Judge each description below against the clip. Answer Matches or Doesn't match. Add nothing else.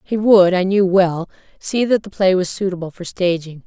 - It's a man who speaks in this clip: Doesn't match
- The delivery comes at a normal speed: Doesn't match